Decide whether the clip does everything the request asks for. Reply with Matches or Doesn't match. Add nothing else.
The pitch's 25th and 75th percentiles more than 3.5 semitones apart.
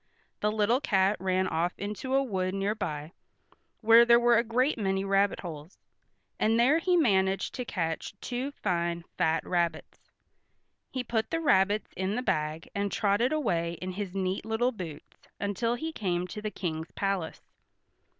Matches